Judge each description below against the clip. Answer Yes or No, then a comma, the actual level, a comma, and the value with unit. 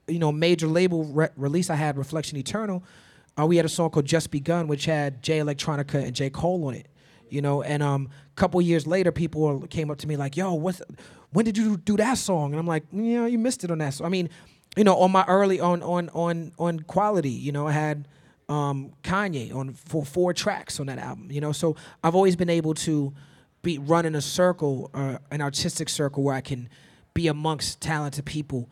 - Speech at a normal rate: No, fast, 225 wpm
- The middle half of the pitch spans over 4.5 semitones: No, average, 3.4 semitones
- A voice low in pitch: No, medium, 160 Hz